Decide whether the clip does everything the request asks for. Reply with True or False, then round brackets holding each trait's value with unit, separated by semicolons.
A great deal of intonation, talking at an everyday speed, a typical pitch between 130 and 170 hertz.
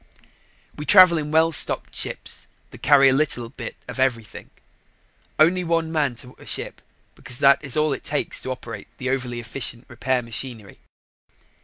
False (4.0 semitones; 165 wpm; 135 Hz)